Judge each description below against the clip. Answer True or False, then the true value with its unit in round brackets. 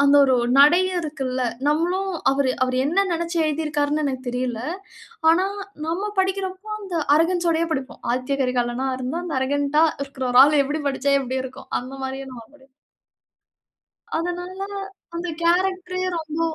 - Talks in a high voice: True (300 Hz)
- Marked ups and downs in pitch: False (4.8 semitones)